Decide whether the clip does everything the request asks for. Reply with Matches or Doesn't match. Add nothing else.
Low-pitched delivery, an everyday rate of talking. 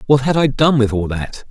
Doesn't match